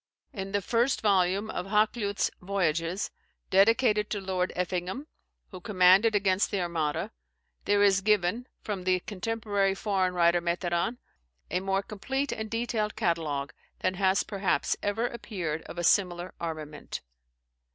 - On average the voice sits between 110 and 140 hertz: No, high, 195 Hz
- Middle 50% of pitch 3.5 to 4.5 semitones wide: No, average, 2.9 semitones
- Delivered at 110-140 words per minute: Yes, slow, 135 wpm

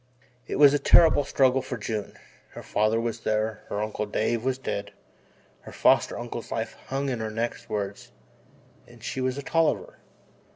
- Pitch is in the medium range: No, low, 115 Hz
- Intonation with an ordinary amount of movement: Yes, average, 3.7 semitones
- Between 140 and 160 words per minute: No, average, 170 wpm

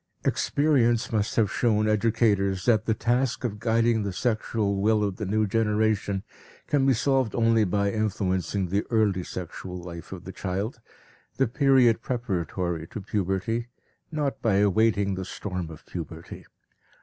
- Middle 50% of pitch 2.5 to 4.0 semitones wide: Yes, average, 3.2 semitones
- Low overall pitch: Yes, low, 105 Hz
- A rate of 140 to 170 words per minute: Yes, average, 150 wpm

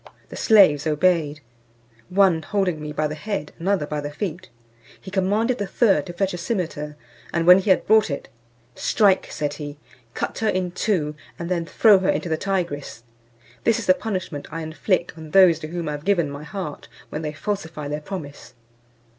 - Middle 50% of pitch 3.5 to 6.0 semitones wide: Yes, average, 4.3 semitones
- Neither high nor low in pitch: Yes, medium, 170 Hz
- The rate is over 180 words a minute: Yes, average, 190 wpm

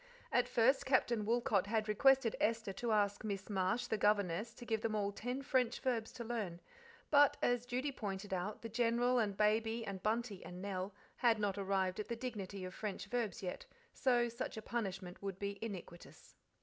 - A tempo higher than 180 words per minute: Yes, average, 190 wpm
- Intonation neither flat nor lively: Yes, average, 3.3 semitones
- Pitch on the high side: Yes, high, 215 Hz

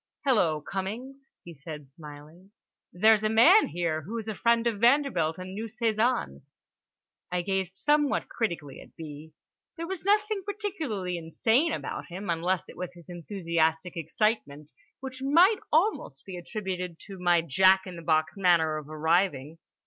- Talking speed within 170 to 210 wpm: No, average, 155 wpm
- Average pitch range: No, wide, 6.3 semitones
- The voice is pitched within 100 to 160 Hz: No, medium, 185 Hz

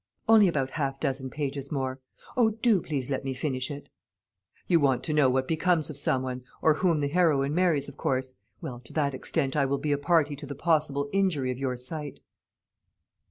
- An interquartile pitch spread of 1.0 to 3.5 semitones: Yes, average, 3.1 semitones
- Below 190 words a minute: No, fast, 205 wpm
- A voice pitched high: No, medium, 145 Hz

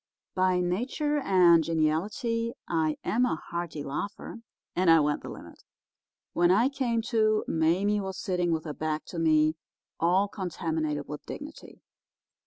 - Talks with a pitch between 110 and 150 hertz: No, medium, 180 Hz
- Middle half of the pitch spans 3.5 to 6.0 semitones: Yes, average, 5.2 semitones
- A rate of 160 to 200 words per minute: No, average, 145 wpm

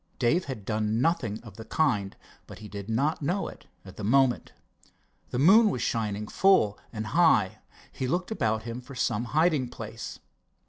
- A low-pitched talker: Yes, low, 120 Hz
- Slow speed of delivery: No, average, 175 wpm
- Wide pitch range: Yes, wide, 5.7 semitones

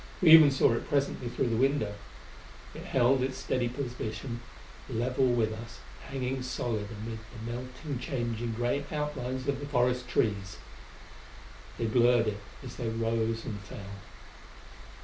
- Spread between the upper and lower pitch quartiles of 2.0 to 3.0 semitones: Yes, narrow, 2.5 semitones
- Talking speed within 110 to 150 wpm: Yes, average, 145 wpm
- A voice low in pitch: Yes, low, 120 Hz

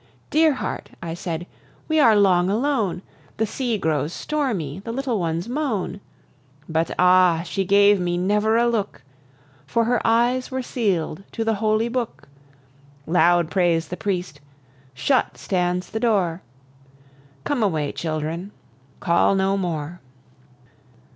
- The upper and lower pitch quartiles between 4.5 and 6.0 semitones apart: Yes, average, 4.9 semitones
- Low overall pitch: No, high, 195 Hz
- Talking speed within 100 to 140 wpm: Yes, slow, 135 wpm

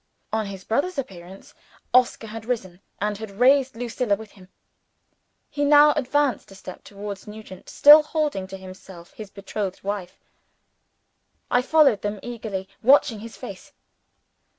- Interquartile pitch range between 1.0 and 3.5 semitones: No, average, 5.0 semitones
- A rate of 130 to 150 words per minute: Yes, average, 140 wpm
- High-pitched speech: Yes, high, 220 Hz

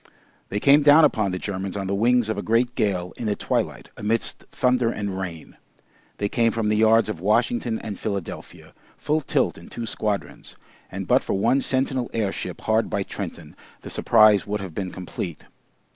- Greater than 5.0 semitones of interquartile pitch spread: No, average, 3.2 semitones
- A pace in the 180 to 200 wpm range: Yes, average, 185 wpm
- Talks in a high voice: No, low, 110 Hz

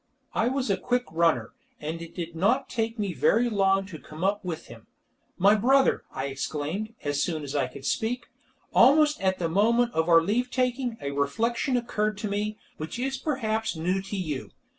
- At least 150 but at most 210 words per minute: Yes, average, 190 wpm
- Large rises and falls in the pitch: Yes, wide, 6.5 semitones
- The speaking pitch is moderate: No, high, 200 Hz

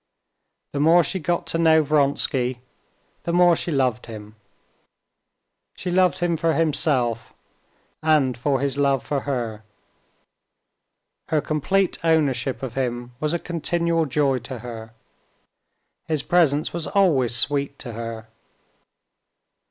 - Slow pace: Yes, slow, 125 wpm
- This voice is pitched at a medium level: Yes, medium, 145 Hz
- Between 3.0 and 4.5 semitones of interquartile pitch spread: No, average, 5.0 semitones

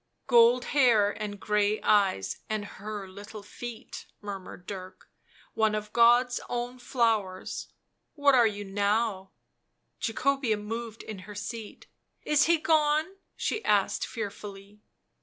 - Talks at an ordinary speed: Yes, average, 150 wpm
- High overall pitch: Yes, high, 215 Hz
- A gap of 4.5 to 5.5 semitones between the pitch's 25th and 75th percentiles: No, average, 3.1 semitones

